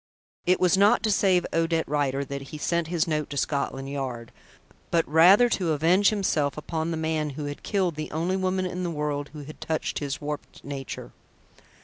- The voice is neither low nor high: Yes, medium, 160 Hz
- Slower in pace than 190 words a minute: No, average, 195 wpm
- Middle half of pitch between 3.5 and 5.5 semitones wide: Yes, average, 3.8 semitones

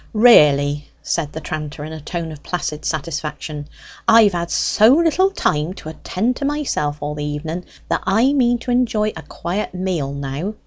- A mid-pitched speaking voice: Yes, medium, 165 Hz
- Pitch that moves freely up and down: Yes, wide, 6.7 semitones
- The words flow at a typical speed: Yes, average, 175 wpm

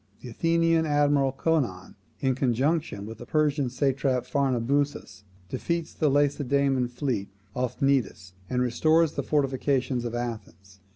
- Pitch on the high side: No, low, 135 Hz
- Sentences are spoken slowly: Yes, slow, 125 wpm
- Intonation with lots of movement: No, average, 3.2 semitones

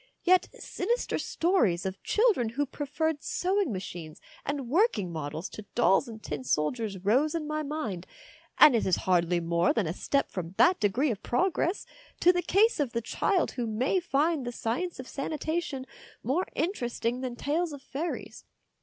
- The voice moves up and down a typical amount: No, wide, 8.0 semitones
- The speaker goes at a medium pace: Yes, average, 170 wpm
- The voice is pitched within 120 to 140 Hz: No, very high, 260 Hz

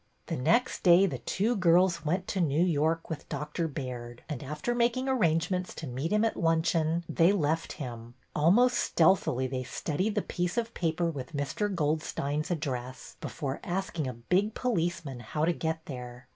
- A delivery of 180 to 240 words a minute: No, average, 170 wpm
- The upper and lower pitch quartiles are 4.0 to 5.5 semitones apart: Yes, average, 4.6 semitones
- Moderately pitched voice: Yes, medium, 160 Hz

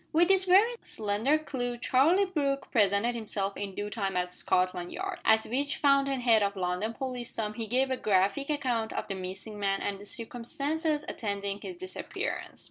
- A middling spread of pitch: No, wide, 5.8 semitones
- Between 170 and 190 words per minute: Yes, average, 175 wpm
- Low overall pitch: No, high, 230 Hz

